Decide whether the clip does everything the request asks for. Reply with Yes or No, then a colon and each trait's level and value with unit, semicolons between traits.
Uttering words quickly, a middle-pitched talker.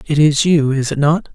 Yes: fast, 225 wpm; medium, 150 Hz